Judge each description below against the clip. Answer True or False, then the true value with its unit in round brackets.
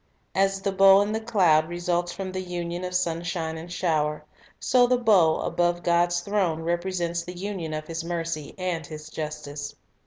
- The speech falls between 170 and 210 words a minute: True (175 wpm)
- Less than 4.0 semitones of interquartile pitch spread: True (2.6 semitones)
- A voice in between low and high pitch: True (175 Hz)